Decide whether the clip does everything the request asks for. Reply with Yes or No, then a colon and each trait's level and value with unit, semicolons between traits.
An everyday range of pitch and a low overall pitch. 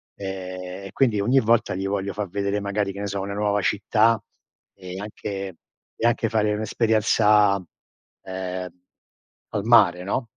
No: narrow, 2.0 semitones; low, 100 Hz